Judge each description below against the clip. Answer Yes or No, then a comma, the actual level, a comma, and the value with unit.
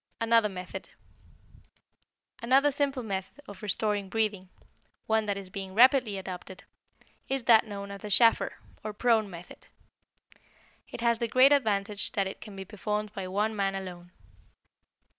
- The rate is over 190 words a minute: No, average, 145 wpm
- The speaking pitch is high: Yes, high, 210 Hz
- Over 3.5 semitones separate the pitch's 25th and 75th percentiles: No, average, 2.9 semitones